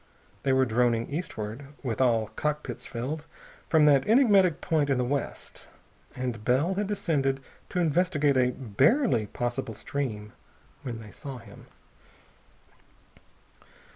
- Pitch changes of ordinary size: Yes, average, 4.6 semitones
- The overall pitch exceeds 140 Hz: No, low, 135 Hz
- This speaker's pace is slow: Yes, slow, 125 wpm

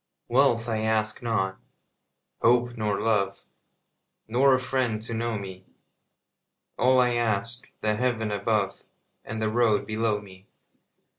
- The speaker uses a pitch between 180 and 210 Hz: No, low, 110 Hz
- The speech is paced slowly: Yes, slow, 130 wpm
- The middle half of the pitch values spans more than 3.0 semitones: No, narrow, 2.4 semitones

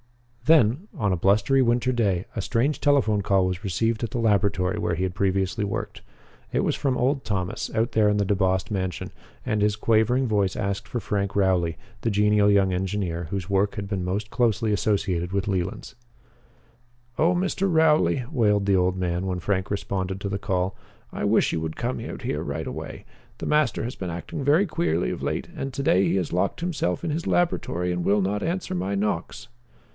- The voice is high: No, low, 100 Hz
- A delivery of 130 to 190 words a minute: No, average, 200 wpm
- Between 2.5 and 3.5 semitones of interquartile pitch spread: No, average, 4.0 semitones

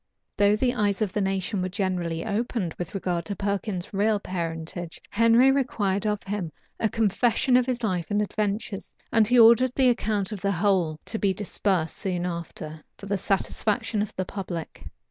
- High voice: Yes, high, 200 Hz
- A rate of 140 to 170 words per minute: No, average, 180 wpm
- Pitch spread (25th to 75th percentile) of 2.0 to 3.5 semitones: Yes, average, 3.2 semitones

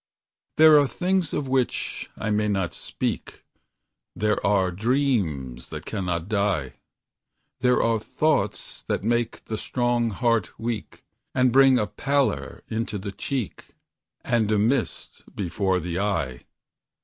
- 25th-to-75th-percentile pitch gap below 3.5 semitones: No, average, 4.6 semitones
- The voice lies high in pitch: No, low, 110 Hz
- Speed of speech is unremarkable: No, slow, 130 wpm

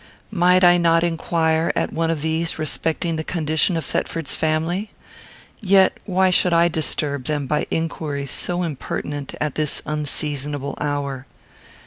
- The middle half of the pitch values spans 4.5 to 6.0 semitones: No, narrow, 2.6 semitones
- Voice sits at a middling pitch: Yes, medium, 160 Hz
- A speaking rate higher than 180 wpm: No, average, 140 wpm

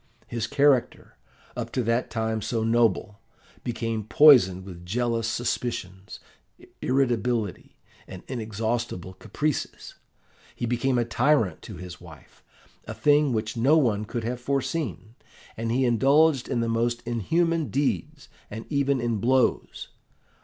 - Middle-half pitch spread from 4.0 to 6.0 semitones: No, average, 3.3 semitones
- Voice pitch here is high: No, low, 120 Hz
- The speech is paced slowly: Yes, slow, 125 wpm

